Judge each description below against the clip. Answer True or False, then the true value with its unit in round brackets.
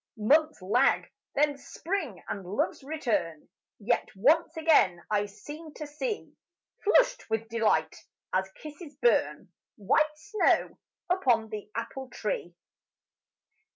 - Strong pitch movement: True (6.9 semitones)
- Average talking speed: False (115 wpm)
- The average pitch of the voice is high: True (275 Hz)